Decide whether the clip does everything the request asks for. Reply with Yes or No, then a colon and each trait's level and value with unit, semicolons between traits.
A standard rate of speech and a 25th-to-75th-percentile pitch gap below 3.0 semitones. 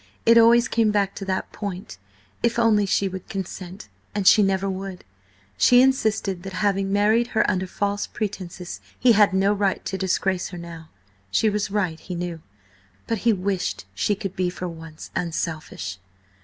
Yes: average, 170 wpm; narrow, 2.5 semitones